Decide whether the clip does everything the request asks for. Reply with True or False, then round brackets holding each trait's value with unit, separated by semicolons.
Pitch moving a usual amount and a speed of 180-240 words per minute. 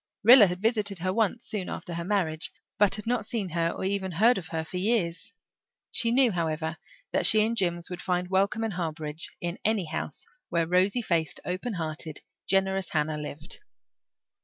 True (4.0 semitones; 185 wpm)